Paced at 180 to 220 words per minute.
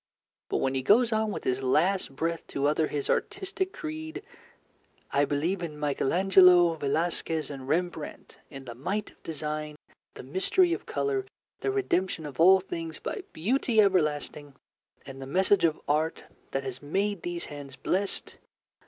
No: average, 160 wpm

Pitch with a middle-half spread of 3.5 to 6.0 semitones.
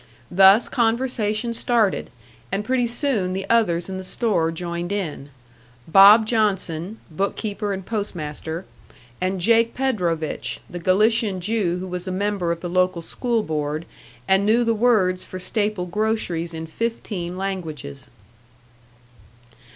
Yes: average, 4.2 semitones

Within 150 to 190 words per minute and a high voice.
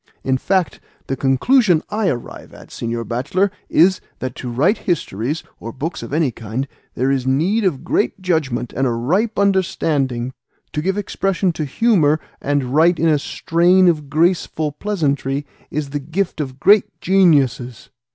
No: average, 160 wpm; medium, 150 Hz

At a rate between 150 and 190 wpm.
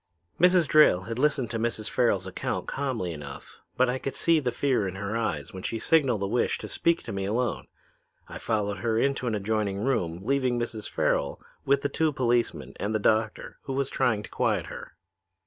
No: average, 200 wpm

